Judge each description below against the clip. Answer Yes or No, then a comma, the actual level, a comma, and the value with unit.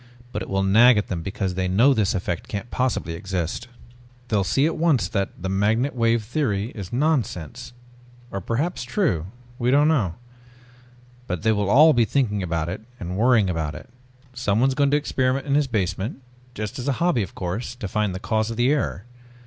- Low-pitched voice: Yes, low, 110 Hz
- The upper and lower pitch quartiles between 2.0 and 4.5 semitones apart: No, average, 5.2 semitones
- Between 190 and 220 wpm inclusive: Yes, average, 195 wpm